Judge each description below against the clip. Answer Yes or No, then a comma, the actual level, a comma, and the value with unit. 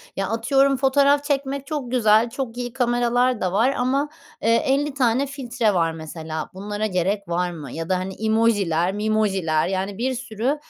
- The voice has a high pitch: Yes, high, 225 Hz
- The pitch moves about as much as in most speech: No, wide, 5.7 semitones